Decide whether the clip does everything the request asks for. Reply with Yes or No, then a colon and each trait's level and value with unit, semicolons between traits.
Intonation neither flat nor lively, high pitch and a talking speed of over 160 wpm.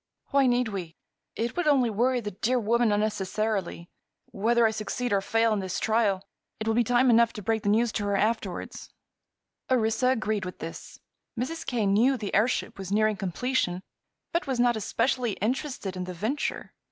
Yes: average, 3.4 semitones; high, 220 Hz; average, 180 wpm